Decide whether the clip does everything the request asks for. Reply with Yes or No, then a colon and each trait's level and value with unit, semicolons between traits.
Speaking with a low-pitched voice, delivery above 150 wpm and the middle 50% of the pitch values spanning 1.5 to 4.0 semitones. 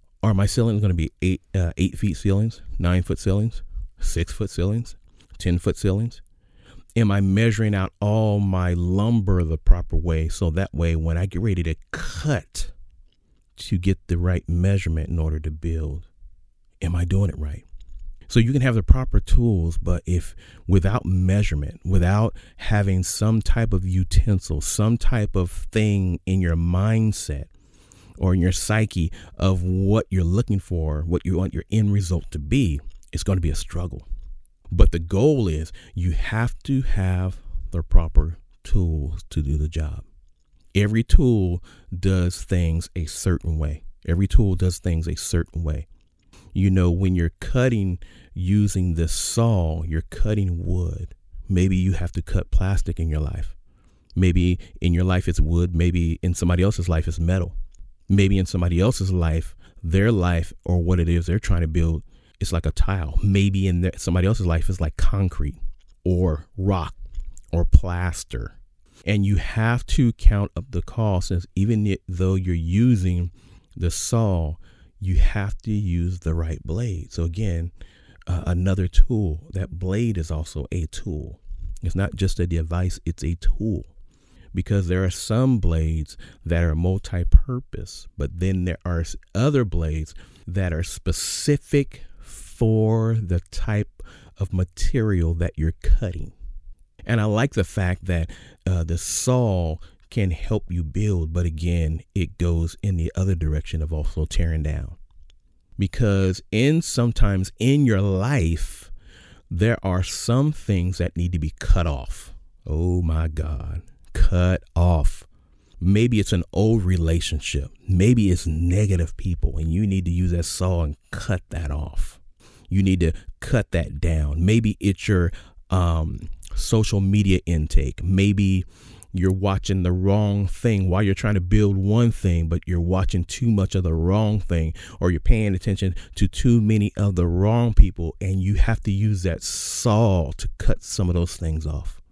Yes: very low, 90 Hz; average, 165 wpm; average, 3.2 semitones